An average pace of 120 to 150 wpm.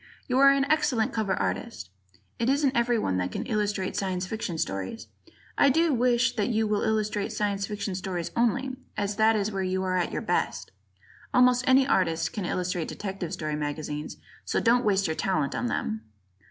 No: average, 180 wpm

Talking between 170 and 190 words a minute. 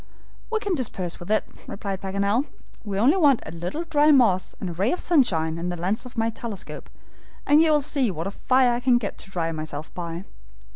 No: fast, 205 wpm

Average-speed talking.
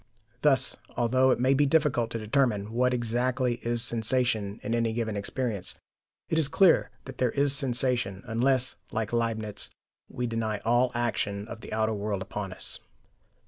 Yes: average, 160 wpm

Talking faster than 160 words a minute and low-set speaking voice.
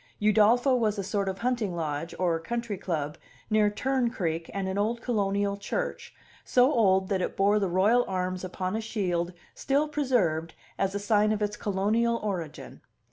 No: average, 175 wpm; high, 205 Hz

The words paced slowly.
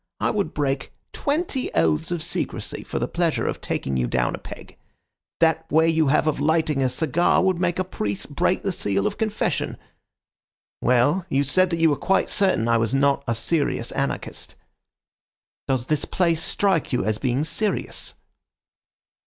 No: average, 170 wpm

